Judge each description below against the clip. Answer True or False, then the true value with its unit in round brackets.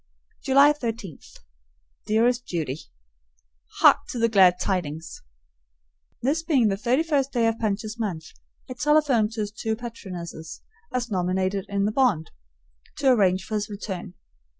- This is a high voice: True (215 Hz)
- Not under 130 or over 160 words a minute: True (140 wpm)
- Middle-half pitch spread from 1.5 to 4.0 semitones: False (4.7 semitones)